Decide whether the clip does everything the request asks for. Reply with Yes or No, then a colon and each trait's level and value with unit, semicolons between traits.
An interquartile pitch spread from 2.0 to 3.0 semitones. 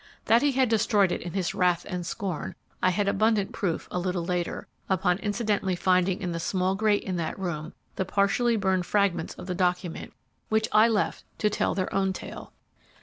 Yes: average, 2.7 semitones